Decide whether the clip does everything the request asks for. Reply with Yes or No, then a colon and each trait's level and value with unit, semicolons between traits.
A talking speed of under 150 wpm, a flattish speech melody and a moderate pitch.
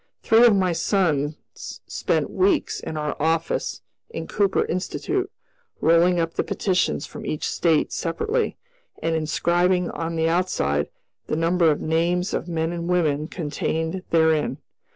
Yes: average, 140 wpm; narrow, 2.2 semitones; medium, 170 Hz